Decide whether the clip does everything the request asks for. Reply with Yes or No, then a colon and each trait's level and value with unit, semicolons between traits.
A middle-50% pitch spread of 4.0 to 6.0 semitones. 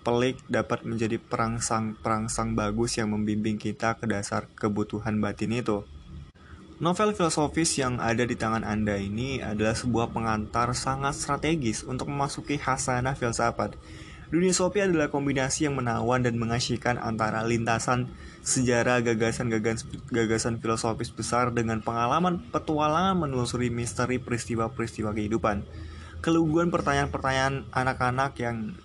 No: average, 3.3 semitones